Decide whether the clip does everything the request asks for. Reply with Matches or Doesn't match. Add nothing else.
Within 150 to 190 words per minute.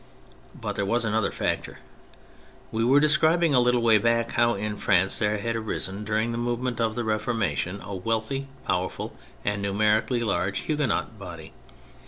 Matches